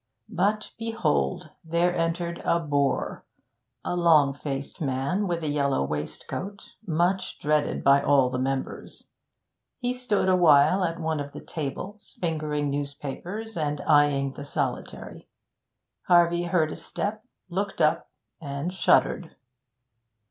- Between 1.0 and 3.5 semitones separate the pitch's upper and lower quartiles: No, average, 4.0 semitones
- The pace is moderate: No, slow, 125 wpm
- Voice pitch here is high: No, medium, 160 Hz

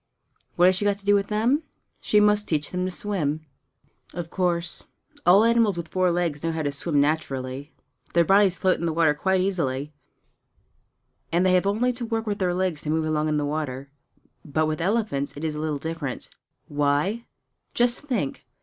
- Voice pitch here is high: No, medium, 170 Hz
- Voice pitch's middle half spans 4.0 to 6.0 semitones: Yes, average, 4.8 semitones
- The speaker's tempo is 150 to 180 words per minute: No, average, 190 wpm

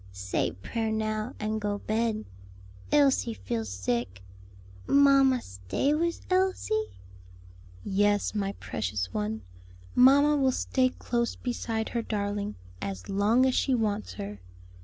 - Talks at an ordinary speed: No, slow, 120 wpm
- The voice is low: No, high, 215 Hz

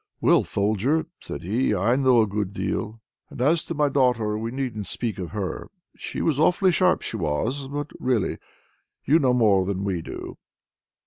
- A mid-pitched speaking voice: No, low, 115 Hz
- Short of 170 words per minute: No, average, 180 wpm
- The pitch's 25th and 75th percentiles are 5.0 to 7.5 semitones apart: Yes, average, 5.3 semitones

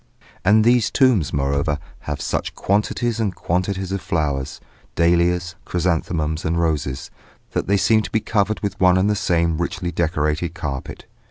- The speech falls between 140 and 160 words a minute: Yes, average, 155 wpm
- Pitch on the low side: Yes, very low, 85 Hz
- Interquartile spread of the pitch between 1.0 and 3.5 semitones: No, average, 4.2 semitones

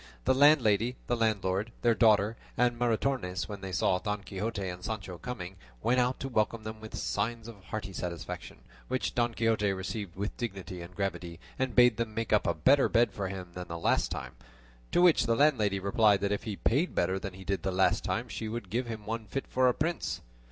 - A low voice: Yes, low, 110 Hz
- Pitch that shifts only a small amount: No, average, 3.7 semitones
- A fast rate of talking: Yes, fast, 215 wpm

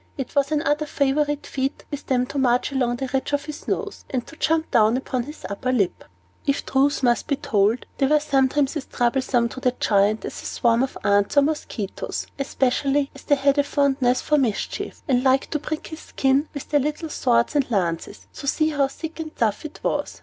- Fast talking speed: Yes, fast, 210 wpm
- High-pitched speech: Yes, very high, 270 Hz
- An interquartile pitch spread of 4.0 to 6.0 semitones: No, average, 3.0 semitones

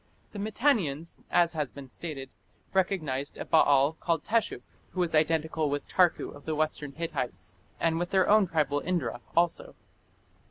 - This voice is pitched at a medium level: Yes, medium, 160 Hz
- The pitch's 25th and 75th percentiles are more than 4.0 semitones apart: No, average, 3.7 semitones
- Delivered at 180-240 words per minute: No, average, 155 wpm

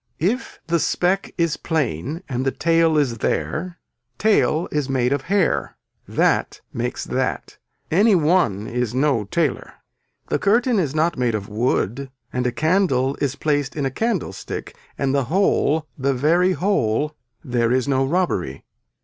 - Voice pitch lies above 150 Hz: No, medium, 145 Hz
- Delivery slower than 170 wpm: Yes, average, 150 wpm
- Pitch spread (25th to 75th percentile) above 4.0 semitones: Yes, average, 5.2 semitones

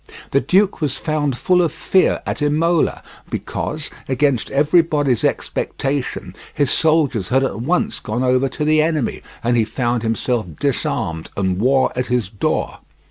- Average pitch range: Yes, average, 4.3 semitones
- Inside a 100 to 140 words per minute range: No, average, 150 wpm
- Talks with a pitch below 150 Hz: Yes, low, 135 Hz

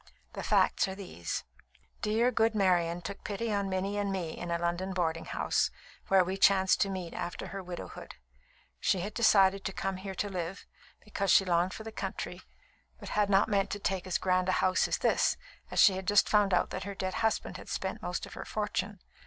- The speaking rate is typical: No, fast, 210 wpm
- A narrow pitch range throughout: Yes, narrow, 1.9 semitones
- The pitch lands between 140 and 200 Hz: Yes, high, 190 Hz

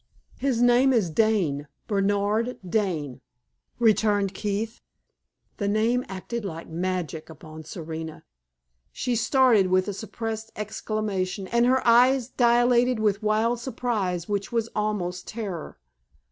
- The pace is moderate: No, slow, 120 wpm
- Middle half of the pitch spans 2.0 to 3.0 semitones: No, average, 4.2 semitones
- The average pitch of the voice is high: Yes, high, 215 Hz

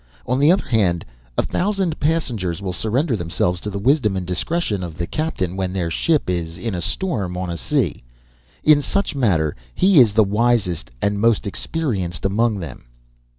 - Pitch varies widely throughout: Yes, wide, 7.5 semitones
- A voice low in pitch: Yes, low, 100 Hz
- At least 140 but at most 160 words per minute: No, average, 180 wpm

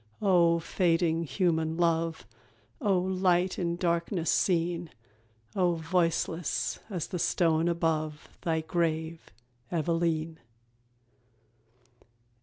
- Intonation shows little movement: Yes, narrow, 1.5 semitones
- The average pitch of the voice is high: No, medium, 170 Hz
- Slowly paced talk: Yes, slow, 85 wpm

